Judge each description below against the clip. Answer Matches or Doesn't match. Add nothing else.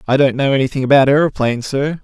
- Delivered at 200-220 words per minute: Matches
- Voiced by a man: Matches